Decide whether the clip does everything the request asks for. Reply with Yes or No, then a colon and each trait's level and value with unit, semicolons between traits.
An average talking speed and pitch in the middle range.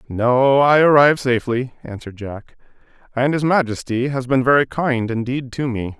No: average, 160 wpm; low, 125 Hz